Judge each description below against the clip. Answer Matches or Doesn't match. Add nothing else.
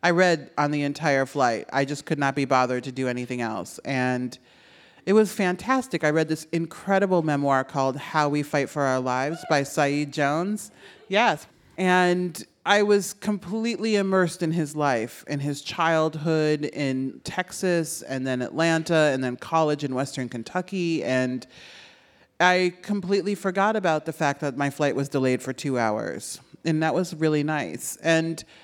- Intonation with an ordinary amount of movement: Matches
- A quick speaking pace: Doesn't match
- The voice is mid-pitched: Matches